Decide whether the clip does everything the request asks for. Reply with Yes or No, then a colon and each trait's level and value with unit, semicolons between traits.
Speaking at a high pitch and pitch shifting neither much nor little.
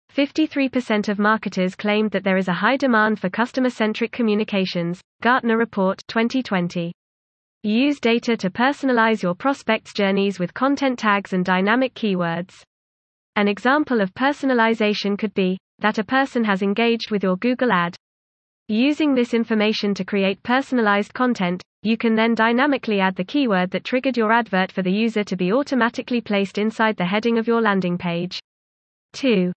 Yes: high, 215 Hz; average, 4.3 semitones